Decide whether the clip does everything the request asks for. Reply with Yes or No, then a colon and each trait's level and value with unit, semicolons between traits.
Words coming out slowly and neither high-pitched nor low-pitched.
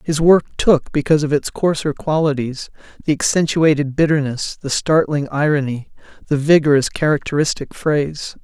Yes: slow, 130 wpm; medium, 150 Hz